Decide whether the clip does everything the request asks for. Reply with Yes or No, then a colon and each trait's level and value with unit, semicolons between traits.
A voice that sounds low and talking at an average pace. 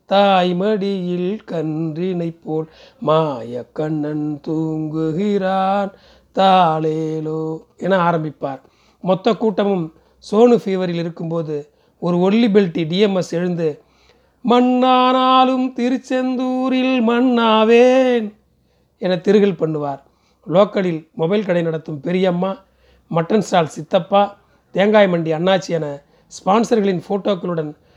No: medium, 185 Hz; average, 85 wpm